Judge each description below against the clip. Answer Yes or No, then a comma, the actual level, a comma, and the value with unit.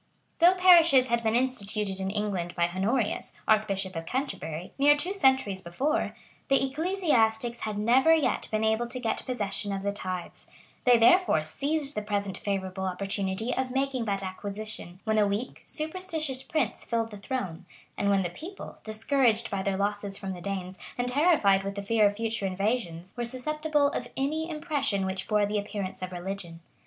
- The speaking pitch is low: No, high, 215 Hz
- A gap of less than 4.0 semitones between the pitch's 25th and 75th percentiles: No, average, 5.3 semitones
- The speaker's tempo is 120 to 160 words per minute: No, average, 175 wpm